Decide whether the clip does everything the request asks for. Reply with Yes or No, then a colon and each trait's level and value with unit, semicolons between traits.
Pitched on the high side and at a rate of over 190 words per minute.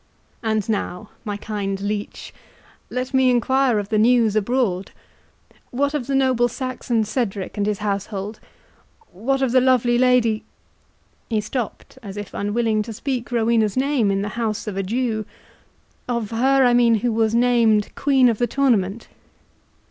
No: high, 230 Hz; average, 150 wpm